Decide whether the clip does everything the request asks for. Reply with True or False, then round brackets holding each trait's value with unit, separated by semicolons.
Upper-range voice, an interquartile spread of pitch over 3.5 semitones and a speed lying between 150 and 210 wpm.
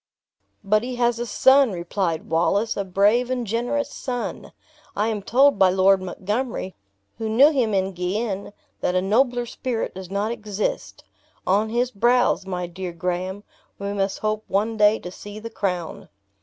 True (210 Hz; 3.9 semitones; 165 wpm)